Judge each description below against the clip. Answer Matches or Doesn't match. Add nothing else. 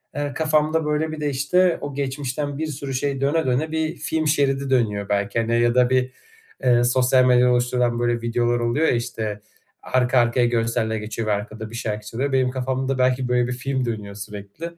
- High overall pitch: Doesn't match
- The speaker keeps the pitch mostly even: Doesn't match